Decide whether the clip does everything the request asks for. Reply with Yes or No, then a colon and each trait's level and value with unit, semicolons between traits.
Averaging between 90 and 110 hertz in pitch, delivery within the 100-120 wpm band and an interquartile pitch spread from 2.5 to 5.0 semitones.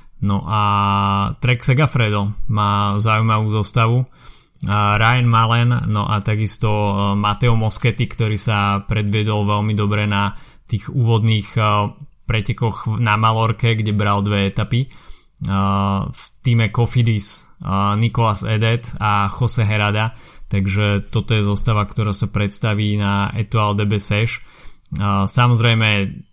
No: low, 105 Hz; slow, 110 wpm; narrow, 2.0 semitones